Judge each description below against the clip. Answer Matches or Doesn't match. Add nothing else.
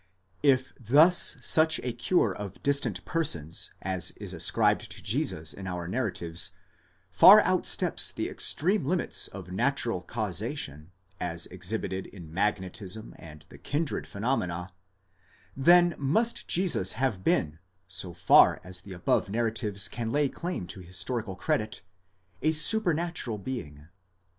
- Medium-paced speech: Doesn't match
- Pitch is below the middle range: Matches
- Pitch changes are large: Matches